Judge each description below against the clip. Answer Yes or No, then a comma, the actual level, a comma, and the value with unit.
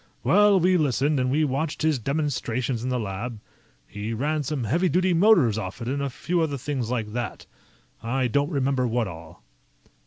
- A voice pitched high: No, low, 135 Hz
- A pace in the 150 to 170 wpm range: No, average, 185 wpm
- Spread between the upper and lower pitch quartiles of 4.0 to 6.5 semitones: Yes, average, 4.9 semitones